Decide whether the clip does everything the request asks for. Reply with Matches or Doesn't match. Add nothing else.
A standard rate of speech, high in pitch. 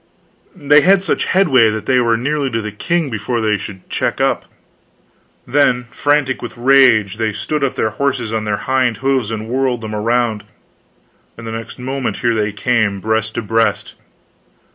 Doesn't match